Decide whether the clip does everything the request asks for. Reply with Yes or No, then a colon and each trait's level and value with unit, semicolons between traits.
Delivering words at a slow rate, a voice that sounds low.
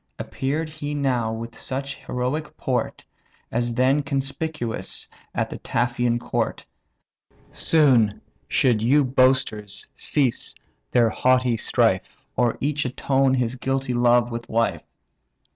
Yes: slow, 115 wpm; low, 125 Hz